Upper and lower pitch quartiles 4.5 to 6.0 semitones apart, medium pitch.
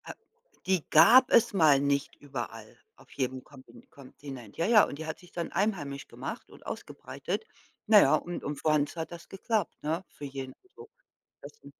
Yes: average, 5.1 semitones; medium, 150 Hz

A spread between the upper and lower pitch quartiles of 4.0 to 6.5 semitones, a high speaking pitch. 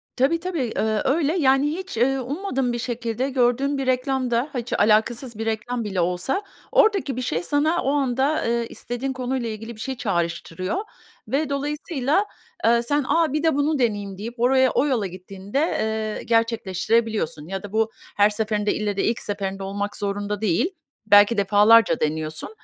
Yes: average, 4.6 semitones; high, 235 Hz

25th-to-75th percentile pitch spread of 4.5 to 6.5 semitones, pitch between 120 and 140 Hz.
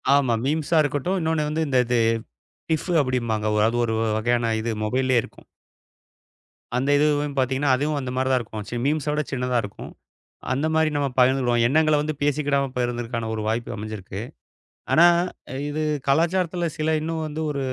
No: average, 4.1 semitones; low, 135 Hz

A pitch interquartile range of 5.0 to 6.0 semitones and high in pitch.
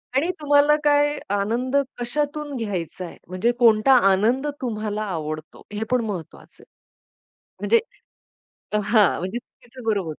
Yes: wide, 5.4 semitones; high, 225 Hz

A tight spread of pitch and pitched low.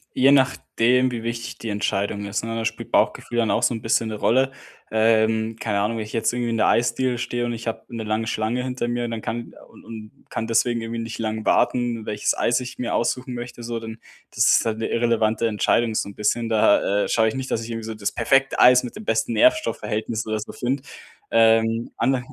Yes: narrow, 1.6 semitones; low, 115 Hz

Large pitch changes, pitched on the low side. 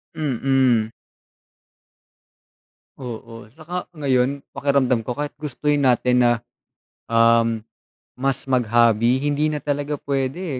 No: average, 3.3 semitones; low, 130 Hz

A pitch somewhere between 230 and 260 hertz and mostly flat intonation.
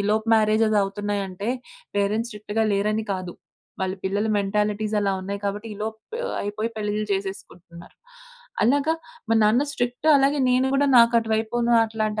No: high, 215 Hz; narrow, 2.0 semitones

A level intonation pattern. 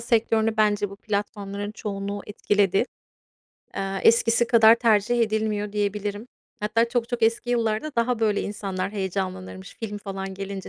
Yes: narrow, 2.3 semitones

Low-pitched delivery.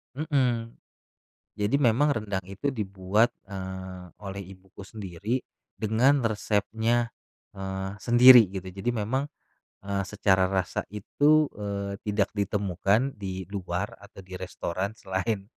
Yes: low, 100 Hz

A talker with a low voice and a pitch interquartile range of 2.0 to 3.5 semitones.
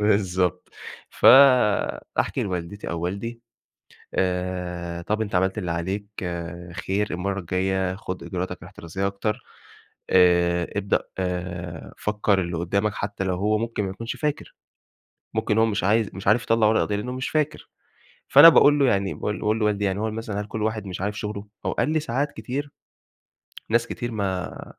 Yes: low, 100 Hz; average, 3.1 semitones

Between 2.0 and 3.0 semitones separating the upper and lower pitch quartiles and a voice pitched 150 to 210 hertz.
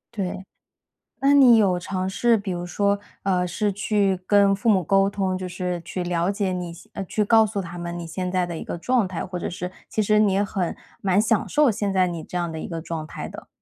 Yes: narrow, 2.5 semitones; high, 190 Hz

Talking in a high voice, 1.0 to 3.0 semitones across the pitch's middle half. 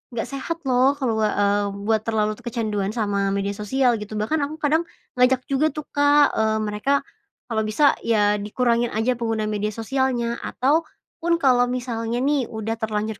No: high, 230 Hz; average, 3.8 semitones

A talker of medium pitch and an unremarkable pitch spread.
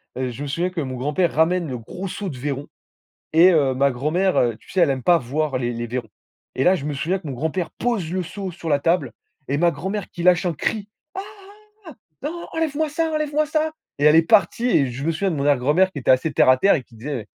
No: medium, 160 Hz; wide, 5.7 semitones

